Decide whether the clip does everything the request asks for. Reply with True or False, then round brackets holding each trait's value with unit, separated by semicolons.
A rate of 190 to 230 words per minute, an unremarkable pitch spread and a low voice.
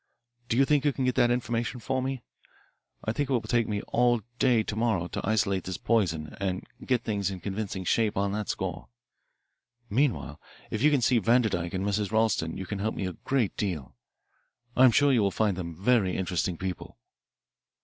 True (200 wpm; 4.3 semitones; 110 Hz)